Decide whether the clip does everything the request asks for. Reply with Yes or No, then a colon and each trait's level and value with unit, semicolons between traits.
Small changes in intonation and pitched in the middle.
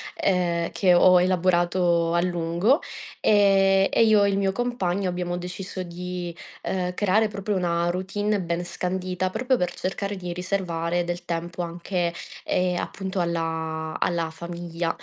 Yes: narrow, 2.0 semitones; medium, 180 Hz